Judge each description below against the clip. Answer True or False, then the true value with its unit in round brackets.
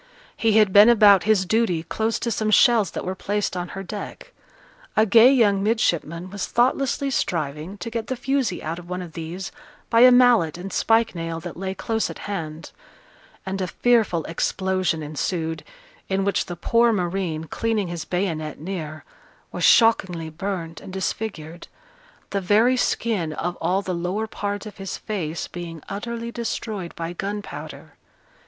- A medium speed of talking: True (165 wpm)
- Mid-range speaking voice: False (195 Hz)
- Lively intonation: False (4.5 semitones)